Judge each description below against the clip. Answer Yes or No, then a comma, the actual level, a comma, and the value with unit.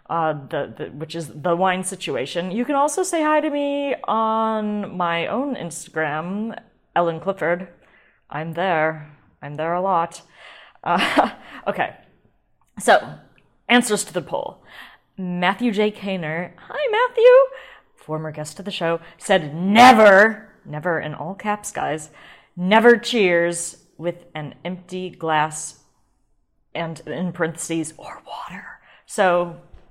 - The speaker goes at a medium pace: No, slow, 125 wpm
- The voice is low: No, medium, 180 Hz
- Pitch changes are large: No, average, 4.5 semitones